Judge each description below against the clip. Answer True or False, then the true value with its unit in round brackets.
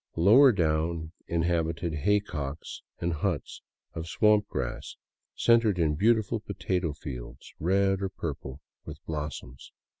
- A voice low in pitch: True (85 Hz)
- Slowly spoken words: True (115 wpm)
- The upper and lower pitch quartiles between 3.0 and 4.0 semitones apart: False (4.5 semitones)